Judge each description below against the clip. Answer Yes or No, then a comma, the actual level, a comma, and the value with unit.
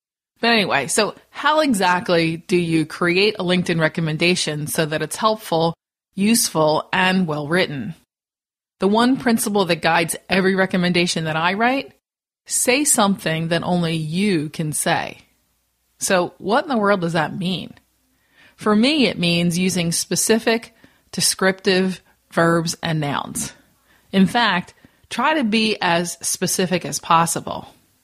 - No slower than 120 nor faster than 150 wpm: Yes, slow, 135 wpm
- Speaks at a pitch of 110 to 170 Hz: No, medium, 180 Hz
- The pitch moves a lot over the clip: No, average, 4.0 semitones